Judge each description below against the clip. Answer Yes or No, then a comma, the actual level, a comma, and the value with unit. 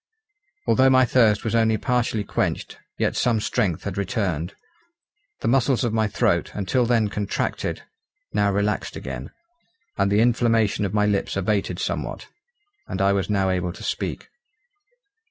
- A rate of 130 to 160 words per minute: Yes, average, 150 wpm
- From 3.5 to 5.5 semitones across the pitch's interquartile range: No, average, 2.8 semitones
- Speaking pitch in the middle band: No, low, 105 Hz